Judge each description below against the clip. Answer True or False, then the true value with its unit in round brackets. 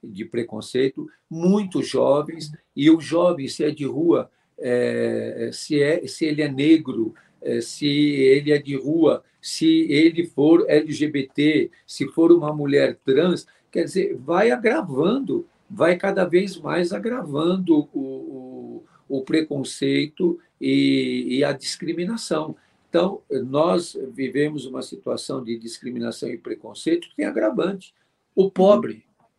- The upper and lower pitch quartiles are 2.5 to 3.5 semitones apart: False (4.3 semitones)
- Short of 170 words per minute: True (130 wpm)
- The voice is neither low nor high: True (150 Hz)